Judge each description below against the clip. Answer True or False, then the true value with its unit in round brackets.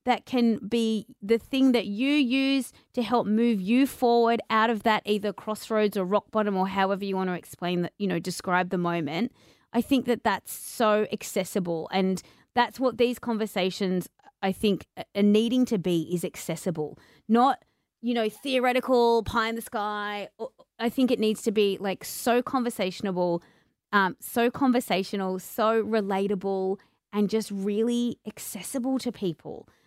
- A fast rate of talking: False (160 wpm)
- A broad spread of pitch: False (3.8 semitones)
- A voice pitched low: False (215 Hz)